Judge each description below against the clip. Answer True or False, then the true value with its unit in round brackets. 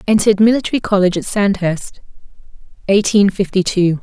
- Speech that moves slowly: True (120 wpm)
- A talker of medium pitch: False (200 Hz)